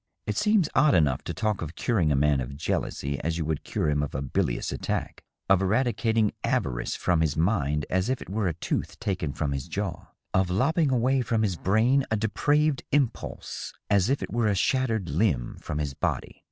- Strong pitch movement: Yes, wide, 7.9 semitones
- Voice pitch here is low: Yes, very low, 95 Hz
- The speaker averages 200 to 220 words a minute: Yes, fast, 205 wpm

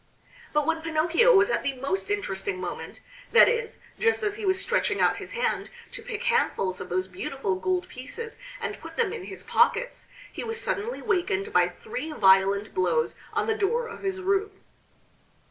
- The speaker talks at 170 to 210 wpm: Yes, average, 180 wpm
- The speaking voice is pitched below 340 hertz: No, very high, 390 Hz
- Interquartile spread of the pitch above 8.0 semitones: Yes, wide, 8.4 semitones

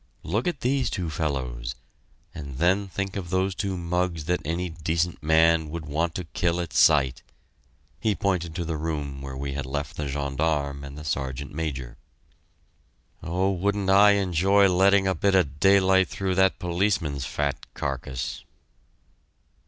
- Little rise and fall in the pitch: No, average, 4.8 semitones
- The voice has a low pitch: Yes, very low, 85 Hz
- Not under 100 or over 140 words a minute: No, average, 155 wpm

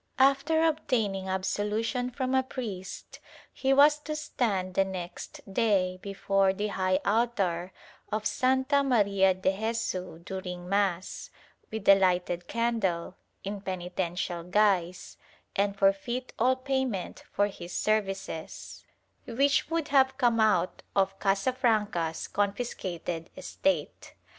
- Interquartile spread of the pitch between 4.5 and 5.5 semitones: Yes, average, 4.9 semitones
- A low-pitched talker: No, high, 200 Hz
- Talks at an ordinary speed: No, slow, 120 wpm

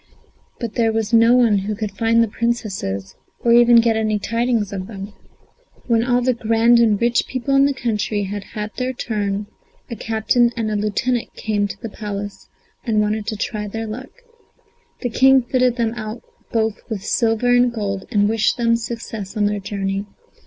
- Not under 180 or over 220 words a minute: Yes, average, 185 wpm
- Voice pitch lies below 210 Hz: No, high, 225 Hz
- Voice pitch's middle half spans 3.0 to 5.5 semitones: No, narrow, 2.4 semitones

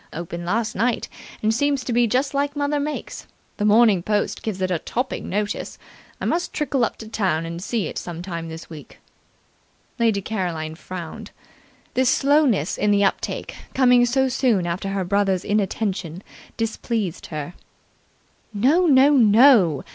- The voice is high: Yes, high, 210 Hz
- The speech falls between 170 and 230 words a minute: No, average, 155 wpm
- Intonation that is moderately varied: No, wide, 5.7 semitones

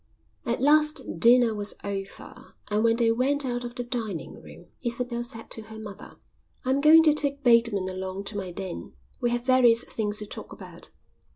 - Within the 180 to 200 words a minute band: Yes, average, 185 wpm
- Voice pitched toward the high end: Yes, high, 235 Hz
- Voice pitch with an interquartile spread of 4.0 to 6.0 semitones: No, average, 3.4 semitones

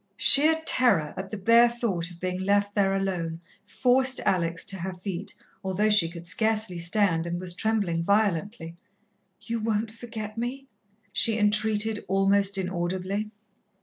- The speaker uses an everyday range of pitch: Yes, average, 3.5 semitones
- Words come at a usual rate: Yes, average, 145 wpm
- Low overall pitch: No, high, 200 Hz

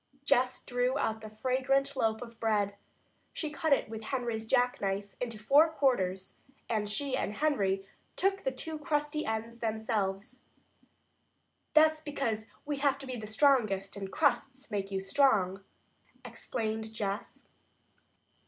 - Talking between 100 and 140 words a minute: Yes, slow, 135 wpm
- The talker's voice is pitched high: Yes, high, 235 Hz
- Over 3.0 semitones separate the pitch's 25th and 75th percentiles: Yes, average, 4.6 semitones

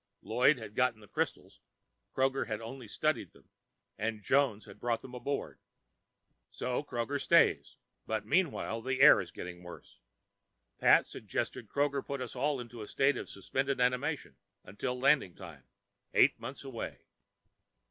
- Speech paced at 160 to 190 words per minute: No, average, 145 wpm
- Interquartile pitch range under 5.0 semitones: Yes, average, 4.0 semitones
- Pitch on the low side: Yes, low, 125 Hz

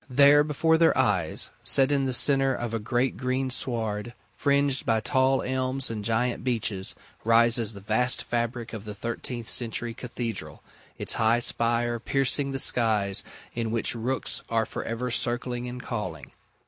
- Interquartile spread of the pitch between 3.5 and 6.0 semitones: No, narrow, 2.6 semitones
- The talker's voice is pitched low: Yes, low, 120 Hz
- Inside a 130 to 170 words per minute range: Yes, average, 160 wpm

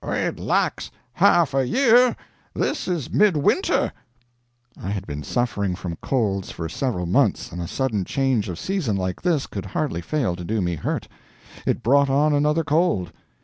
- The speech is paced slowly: No, average, 170 wpm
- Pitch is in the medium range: No, low, 125 Hz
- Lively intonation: Yes, wide, 8.7 semitones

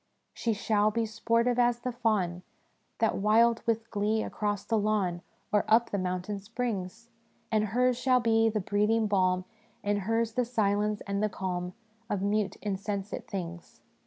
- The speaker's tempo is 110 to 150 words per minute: No, average, 165 wpm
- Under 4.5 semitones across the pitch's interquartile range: Yes, narrow, 2.4 semitones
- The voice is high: Yes, high, 210 Hz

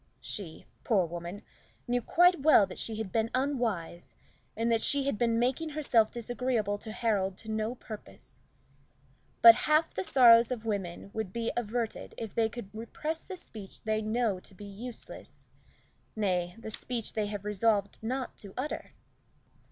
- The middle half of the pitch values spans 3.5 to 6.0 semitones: No, average, 3.1 semitones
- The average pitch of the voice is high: Yes, high, 220 Hz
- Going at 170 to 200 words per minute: No, average, 160 wpm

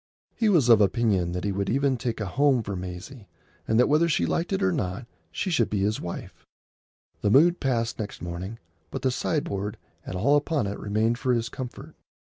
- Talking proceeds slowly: No, fast, 205 wpm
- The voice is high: No, low, 115 Hz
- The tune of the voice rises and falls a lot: Yes, wide, 5.7 semitones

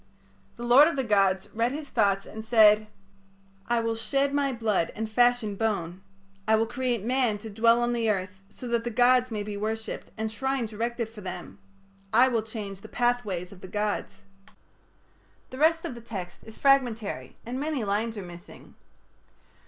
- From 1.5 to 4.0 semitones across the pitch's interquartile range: Yes, average, 2.9 semitones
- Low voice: No, high, 225 Hz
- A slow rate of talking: No, average, 180 wpm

